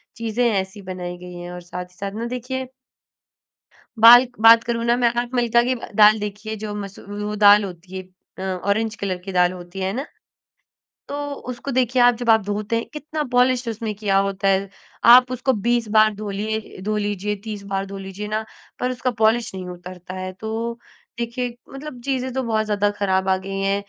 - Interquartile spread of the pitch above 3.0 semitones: Yes, average, 3.6 semitones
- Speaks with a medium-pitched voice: No, high, 215 Hz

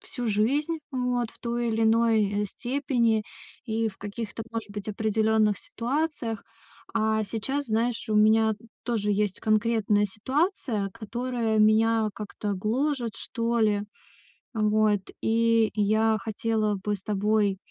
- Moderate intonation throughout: No, narrow, 1.9 semitones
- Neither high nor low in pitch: No, high, 220 Hz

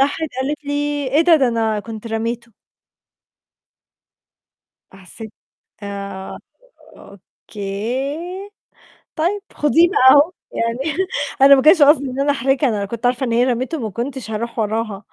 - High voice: Yes, high, 245 Hz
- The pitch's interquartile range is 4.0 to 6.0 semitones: Yes, average, 4.5 semitones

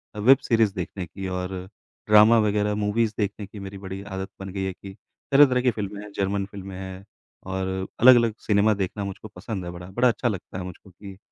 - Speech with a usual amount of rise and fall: No, narrow, 2.0 semitones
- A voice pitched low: Yes, low, 100 Hz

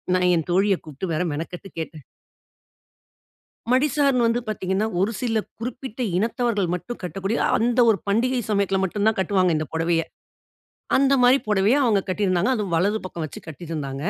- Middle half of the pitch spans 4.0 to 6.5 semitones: Yes, average, 4.7 semitones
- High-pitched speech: Yes, high, 200 Hz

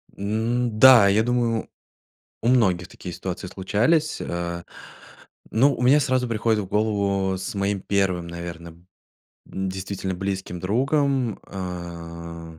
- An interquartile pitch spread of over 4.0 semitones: Yes, average, 4.5 semitones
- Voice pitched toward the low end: Yes, low, 100 Hz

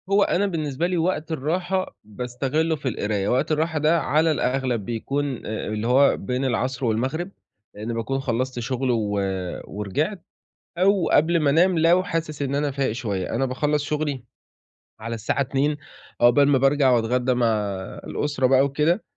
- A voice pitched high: No, low, 135 Hz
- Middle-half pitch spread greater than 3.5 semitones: Yes, average, 4.2 semitones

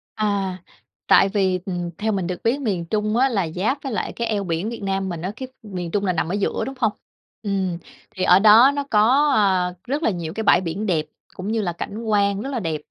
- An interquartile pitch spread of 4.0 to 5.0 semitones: No, average, 3.3 semitones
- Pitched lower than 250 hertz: Yes, high, 200 Hz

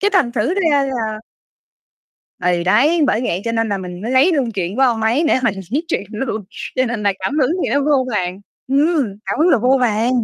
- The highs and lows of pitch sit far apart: No, average, 5.0 semitones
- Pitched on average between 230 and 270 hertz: Yes, high, 240 Hz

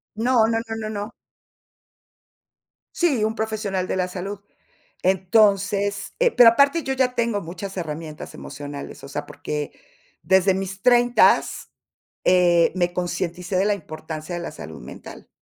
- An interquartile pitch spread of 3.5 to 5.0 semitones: Yes, average, 4.2 semitones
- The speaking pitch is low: No, high, 195 Hz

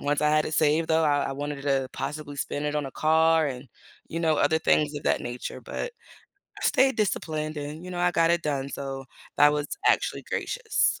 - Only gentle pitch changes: Yes, narrow, 2.1 semitones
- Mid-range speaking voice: Yes, medium, 150 Hz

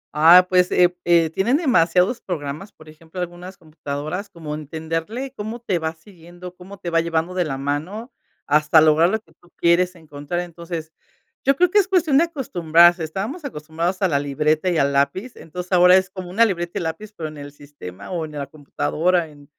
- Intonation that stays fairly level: No, average, 3.3 semitones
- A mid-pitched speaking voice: Yes, medium, 170 Hz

